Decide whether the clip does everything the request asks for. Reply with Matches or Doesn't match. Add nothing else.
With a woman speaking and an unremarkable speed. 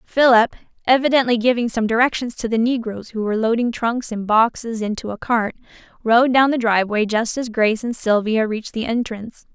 Matches